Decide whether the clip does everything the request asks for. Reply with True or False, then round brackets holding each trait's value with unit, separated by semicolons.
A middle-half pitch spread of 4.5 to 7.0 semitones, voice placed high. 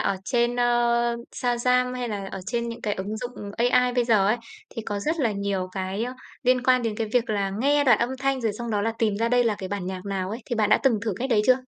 False (3.4 semitones; 230 Hz)